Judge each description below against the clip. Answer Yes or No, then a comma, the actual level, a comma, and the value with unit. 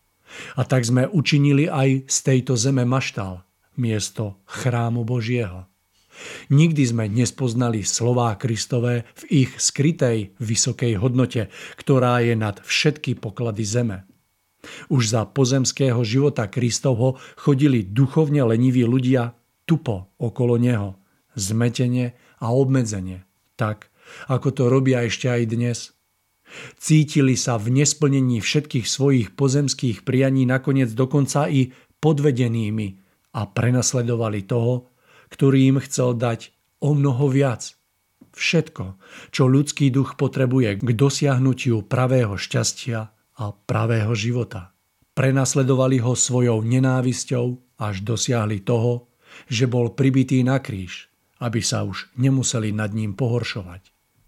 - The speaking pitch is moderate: No, low, 125 Hz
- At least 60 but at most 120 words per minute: Yes, slow, 115 wpm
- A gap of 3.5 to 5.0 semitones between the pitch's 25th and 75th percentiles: No, average, 2.7 semitones